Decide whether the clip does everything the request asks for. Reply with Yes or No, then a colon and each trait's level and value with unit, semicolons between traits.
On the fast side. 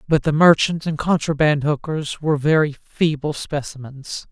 No: average, 140 wpm